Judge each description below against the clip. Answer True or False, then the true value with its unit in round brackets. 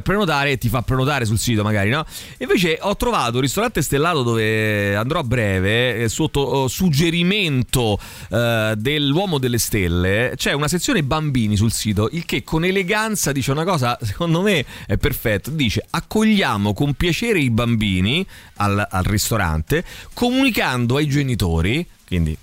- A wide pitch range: True (7.1 semitones)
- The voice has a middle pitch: False (125 Hz)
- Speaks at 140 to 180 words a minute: True (145 wpm)